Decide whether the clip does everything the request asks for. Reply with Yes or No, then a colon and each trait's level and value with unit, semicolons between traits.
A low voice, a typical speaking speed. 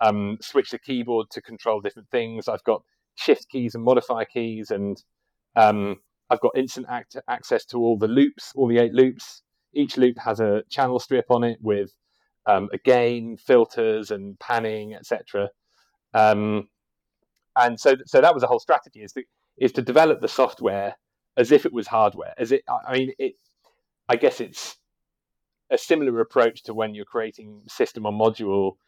Yes: low, 115 Hz; average, 175 wpm